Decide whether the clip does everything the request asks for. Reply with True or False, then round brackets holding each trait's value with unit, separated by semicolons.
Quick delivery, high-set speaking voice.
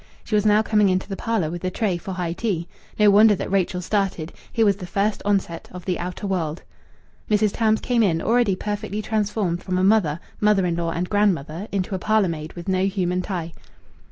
True (215 wpm; 195 Hz)